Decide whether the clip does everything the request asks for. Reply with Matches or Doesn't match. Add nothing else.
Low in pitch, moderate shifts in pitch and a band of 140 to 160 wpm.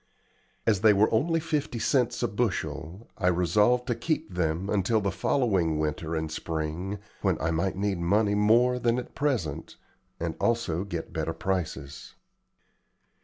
Doesn't match